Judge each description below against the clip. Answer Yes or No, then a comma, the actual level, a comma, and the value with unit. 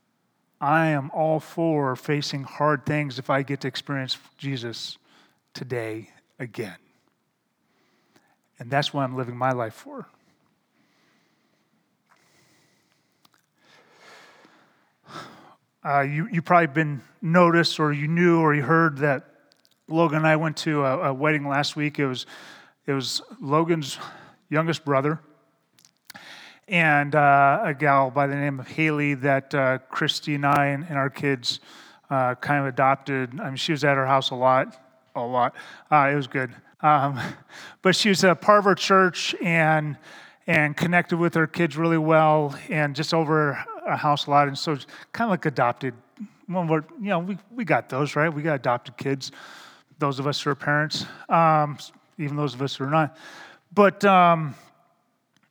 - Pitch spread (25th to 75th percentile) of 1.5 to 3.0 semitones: Yes, average, 2.7 semitones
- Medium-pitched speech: Yes, medium, 145 Hz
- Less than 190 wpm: Yes, average, 160 wpm